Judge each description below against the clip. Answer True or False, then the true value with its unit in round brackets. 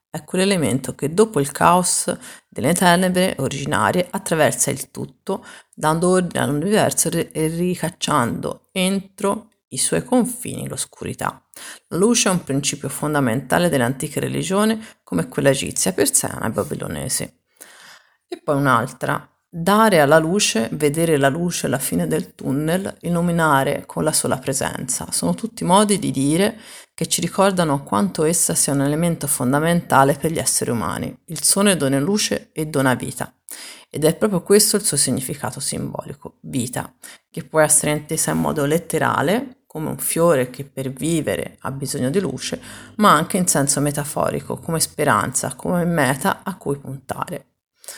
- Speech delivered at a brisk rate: False (145 wpm)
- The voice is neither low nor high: True (160 Hz)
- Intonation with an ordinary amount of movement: True (4.9 semitones)